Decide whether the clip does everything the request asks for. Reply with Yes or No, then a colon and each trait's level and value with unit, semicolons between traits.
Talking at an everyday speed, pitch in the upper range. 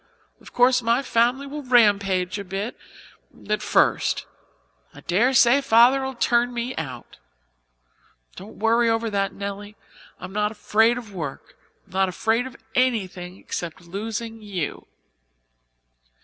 No: slow, 125 wpm; high, 225 Hz